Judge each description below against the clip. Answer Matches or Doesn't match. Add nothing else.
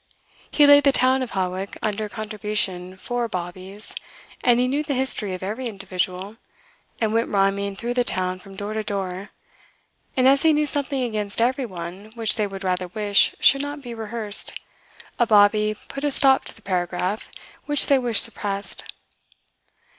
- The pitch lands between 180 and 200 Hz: Doesn't match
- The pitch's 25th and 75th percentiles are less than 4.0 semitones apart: Doesn't match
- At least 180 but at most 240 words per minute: Doesn't match